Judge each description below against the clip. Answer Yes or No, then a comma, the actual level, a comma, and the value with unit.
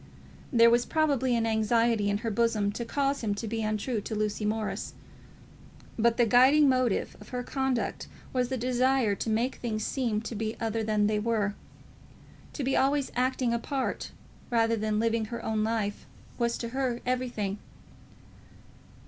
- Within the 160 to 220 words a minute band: Yes, average, 165 wpm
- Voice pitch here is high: Yes, high, 230 Hz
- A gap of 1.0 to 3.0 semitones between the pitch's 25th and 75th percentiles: Yes, average, 2.7 semitones